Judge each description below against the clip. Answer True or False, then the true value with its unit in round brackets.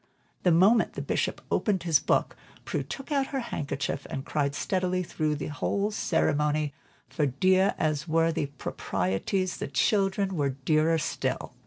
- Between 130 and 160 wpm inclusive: True (155 wpm)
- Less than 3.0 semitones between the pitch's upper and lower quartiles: False (4.7 semitones)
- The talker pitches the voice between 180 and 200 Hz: False (165 Hz)